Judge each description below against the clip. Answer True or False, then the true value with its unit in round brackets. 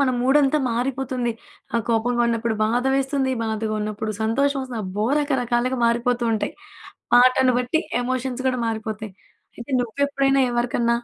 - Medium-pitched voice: False (245 Hz)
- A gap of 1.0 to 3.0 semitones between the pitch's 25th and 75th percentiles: True (2.5 semitones)